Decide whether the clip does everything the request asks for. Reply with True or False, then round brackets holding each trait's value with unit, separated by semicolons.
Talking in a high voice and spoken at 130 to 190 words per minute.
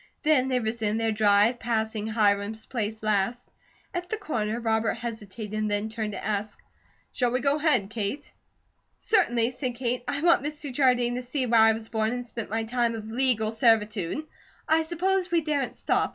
True (230 Hz; 180 wpm)